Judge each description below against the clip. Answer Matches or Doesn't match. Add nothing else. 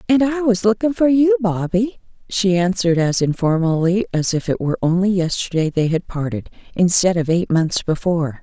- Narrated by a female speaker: Matches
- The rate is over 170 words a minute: Matches